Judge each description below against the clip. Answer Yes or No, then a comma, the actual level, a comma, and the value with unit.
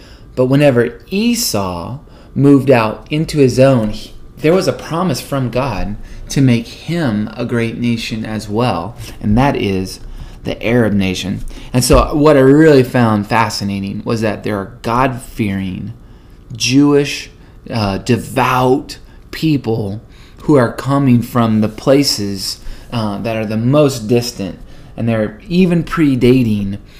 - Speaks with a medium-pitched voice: No, low, 120 Hz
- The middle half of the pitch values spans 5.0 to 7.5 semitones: No, average, 4.1 semitones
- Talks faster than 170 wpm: No, average, 140 wpm